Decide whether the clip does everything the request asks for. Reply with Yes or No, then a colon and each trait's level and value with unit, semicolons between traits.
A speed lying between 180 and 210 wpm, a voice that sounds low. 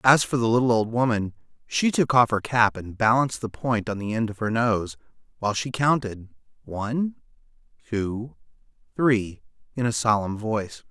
No: average, 170 wpm; low, 115 Hz